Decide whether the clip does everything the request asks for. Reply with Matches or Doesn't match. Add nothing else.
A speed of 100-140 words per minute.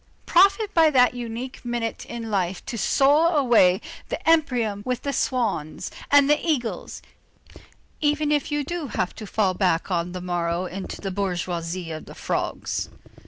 Doesn't match